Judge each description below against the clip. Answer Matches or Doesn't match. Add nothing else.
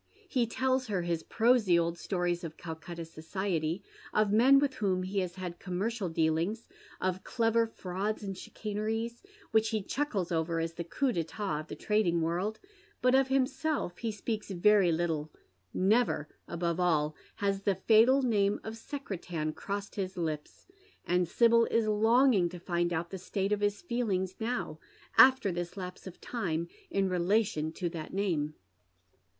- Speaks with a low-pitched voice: Doesn't match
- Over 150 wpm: Matches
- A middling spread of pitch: Matches